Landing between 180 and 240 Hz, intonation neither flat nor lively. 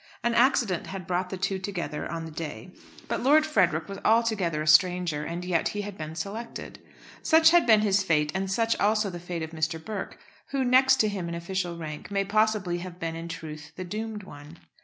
Yes: medium, 185 Hz; average, 4.4 semitones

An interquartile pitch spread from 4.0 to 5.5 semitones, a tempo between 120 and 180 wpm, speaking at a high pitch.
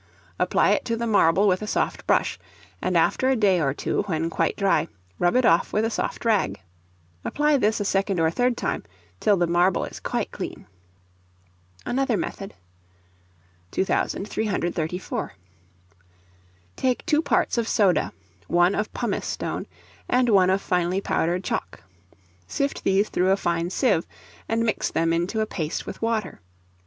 Yes: average, 4.5 semitones; average, 155 wpm; high, 195 Hz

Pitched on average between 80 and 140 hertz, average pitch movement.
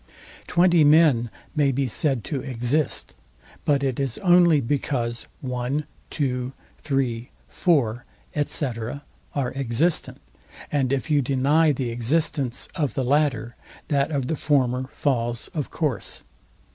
Yes: low, 135 Hz; average, 3.2 semitones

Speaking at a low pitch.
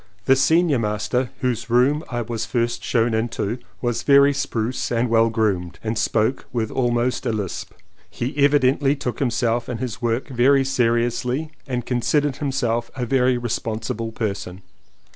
Yes: low, 120 Hz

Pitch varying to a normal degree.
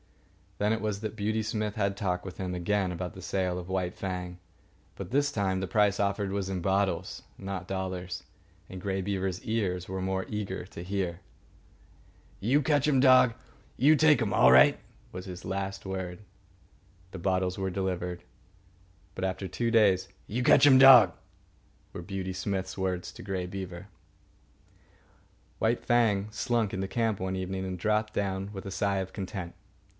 No: narrow, 2.3 semitones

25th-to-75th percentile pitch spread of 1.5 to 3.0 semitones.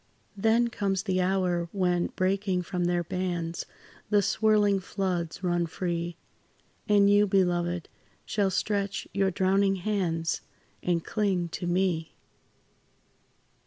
Yes: narrow, 2.4 semitones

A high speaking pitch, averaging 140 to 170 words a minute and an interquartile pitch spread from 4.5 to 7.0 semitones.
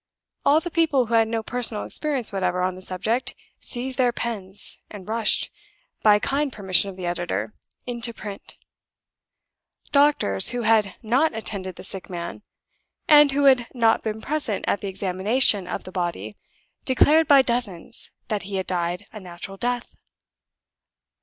Yes: high, 220 Hz; average, 155 wpm; average, 4.9 semitones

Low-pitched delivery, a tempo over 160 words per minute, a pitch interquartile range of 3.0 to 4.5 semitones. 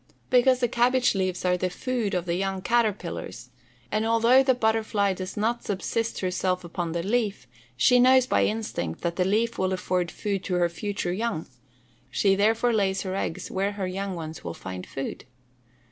No: high, 195 Hz; average, 185 wpm; average, 4.0 semitones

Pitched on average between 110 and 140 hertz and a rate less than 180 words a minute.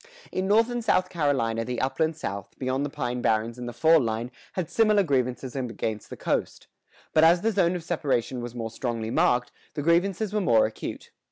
No: low, 135 Hz; average, 195 wpm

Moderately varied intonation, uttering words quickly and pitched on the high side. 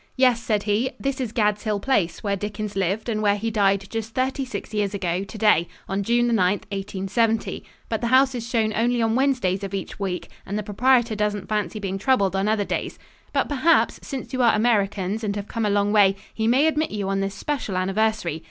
Yes: average, 3.1 semitones; fast, 215 wpm; high, 210 Hz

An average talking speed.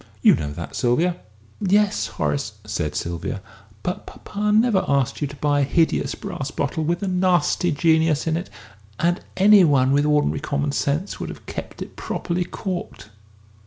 Yes: average, 165 wpm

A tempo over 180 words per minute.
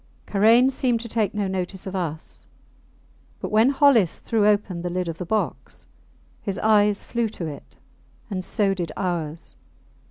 No: average, 160 wpm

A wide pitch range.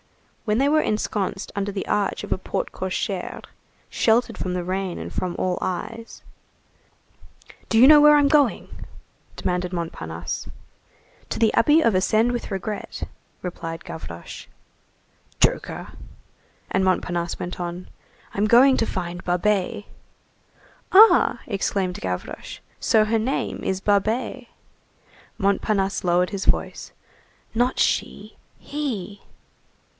No: average, 4.1 semitones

